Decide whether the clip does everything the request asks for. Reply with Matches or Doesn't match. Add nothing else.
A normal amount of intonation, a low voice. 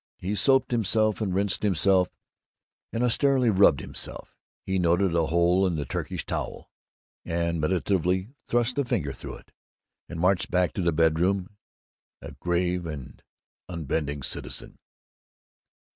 Matches